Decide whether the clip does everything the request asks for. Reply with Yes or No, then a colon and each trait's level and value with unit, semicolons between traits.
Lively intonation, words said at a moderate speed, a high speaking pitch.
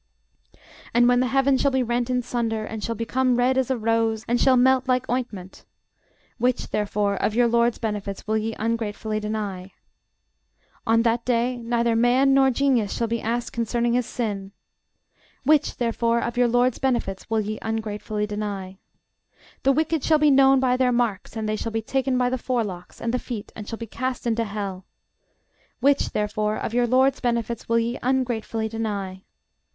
No: average, 2.7 semitones; average, 180 wpm; high, 235 Hz